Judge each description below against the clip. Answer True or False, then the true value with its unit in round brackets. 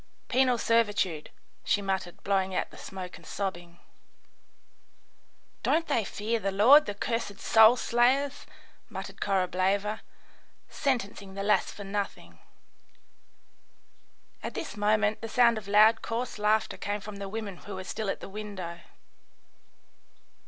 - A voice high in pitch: True (205 Hz)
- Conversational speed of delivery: False (130 wpm)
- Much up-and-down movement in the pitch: False (2.7 semitones)